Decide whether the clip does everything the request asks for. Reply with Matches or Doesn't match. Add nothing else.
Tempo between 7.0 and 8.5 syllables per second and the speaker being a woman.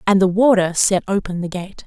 Doesn't match